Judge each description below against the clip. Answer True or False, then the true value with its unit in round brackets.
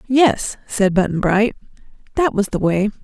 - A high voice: True (210 Hz)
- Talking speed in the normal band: True (160 wpm)